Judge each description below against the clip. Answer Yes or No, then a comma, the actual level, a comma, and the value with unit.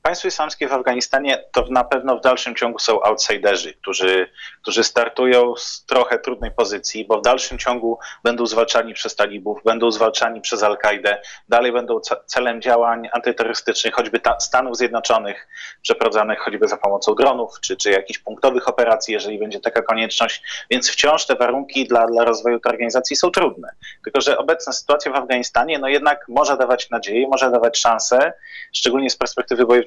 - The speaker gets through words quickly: Yes, fast, 165 wpm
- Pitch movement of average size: No, narrow, 2.3 semitones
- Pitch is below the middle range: Yes, low, 120 Hz